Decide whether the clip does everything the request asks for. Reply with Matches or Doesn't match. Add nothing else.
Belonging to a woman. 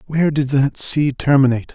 Doesn't match